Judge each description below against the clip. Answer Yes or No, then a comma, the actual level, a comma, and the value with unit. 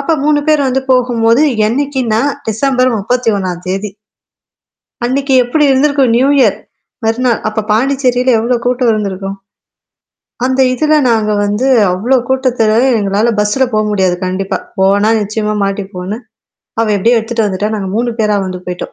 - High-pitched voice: Yes, high, 225 Hz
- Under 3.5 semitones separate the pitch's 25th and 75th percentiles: No, average, 4.1 semitones